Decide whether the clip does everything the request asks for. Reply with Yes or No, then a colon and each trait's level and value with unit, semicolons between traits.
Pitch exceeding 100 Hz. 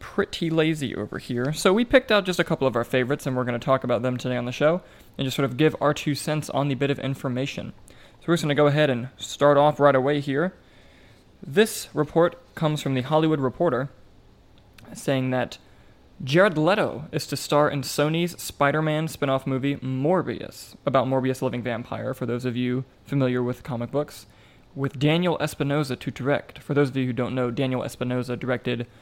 Yes: low, 135 Hz